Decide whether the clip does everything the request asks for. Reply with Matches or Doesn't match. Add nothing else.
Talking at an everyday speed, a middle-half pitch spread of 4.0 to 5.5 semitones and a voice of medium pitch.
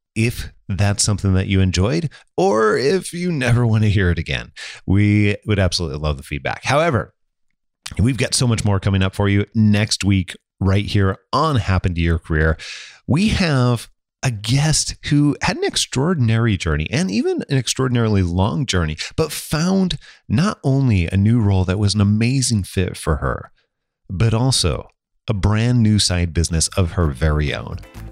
Doesn't match